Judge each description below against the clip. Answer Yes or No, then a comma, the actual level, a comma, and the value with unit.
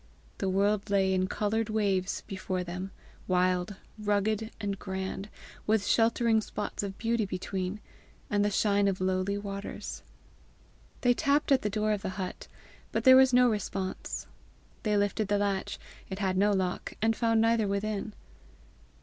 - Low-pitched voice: No, high, 205 Hz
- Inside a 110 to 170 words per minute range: Yes, average, 155 wpm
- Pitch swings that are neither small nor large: No, narrow, 2.3 semitones